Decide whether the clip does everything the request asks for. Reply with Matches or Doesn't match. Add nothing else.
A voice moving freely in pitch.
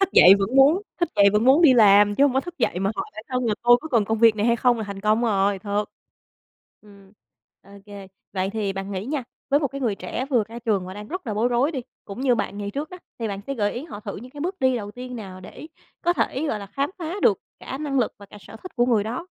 Doesn't match